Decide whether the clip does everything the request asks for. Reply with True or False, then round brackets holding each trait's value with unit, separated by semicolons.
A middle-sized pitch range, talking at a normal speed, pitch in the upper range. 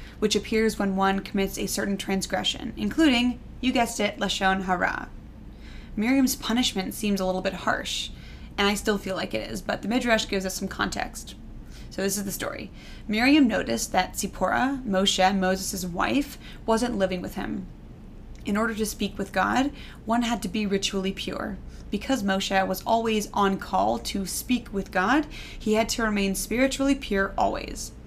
True (3.1 semitones; 170 wpm; 200 Hz)